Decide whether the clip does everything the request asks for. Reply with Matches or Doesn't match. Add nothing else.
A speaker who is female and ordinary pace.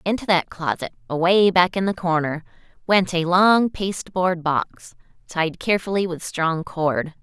Matches